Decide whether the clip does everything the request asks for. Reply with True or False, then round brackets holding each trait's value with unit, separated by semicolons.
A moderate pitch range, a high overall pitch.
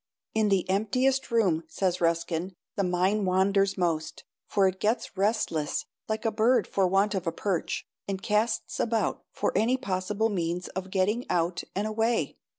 True (3.1 semitones; 195 Hz)